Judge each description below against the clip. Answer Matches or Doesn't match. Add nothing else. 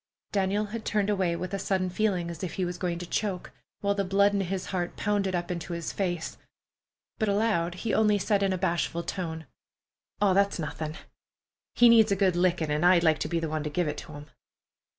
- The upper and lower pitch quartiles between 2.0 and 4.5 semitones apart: Matches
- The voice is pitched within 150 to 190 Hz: Matches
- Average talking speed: Doesn't match